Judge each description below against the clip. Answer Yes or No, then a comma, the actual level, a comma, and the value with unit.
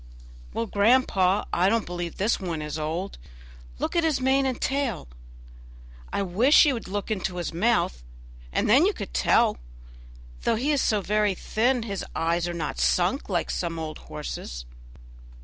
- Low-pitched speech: No, high, 200 Hz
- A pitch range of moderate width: No, wide, 5.9 semitones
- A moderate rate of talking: Yes, average, 170 wpm